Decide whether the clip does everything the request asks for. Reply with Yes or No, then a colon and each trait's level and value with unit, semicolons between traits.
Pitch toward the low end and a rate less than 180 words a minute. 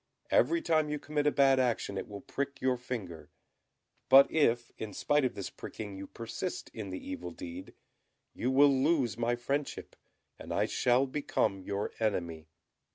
Yes: low, 120 Hz; average, 165 wpm